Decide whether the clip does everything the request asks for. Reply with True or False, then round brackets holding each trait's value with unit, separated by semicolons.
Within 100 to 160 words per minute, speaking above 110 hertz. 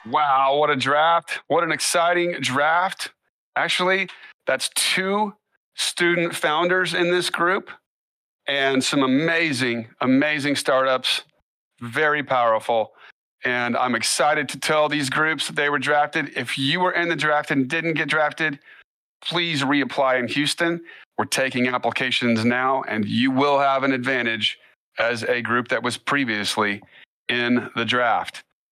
True (140 wpm; 140 Hz)